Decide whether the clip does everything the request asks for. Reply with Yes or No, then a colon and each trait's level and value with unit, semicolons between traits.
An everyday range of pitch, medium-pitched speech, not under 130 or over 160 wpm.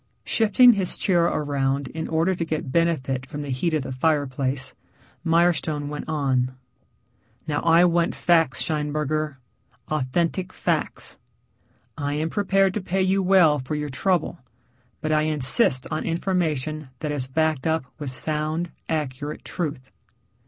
Yes: average, 3.1 semitones; medium, 155 Hz; average, 140 wpm